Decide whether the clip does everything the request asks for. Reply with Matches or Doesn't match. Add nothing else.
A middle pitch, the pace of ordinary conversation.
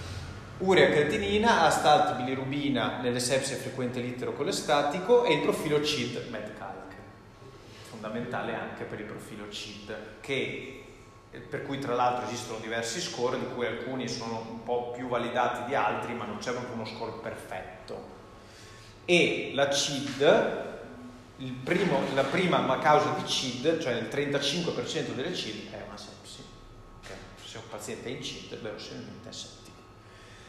Doesn't match